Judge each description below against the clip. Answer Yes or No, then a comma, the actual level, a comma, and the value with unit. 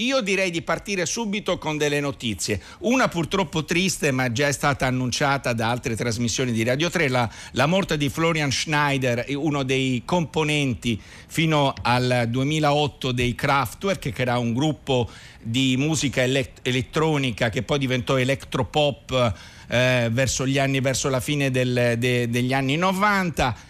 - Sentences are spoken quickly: No, average, 150 wpm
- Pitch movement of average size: Yes, average, 3.7 semitones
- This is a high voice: No, low, 135 Hz